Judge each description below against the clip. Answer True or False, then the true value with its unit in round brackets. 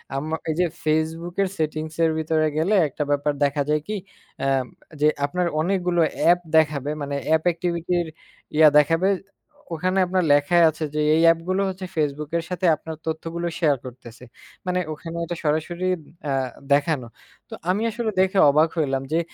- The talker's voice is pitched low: False (160 Hz)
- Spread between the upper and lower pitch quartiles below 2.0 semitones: False (2.7 semitones)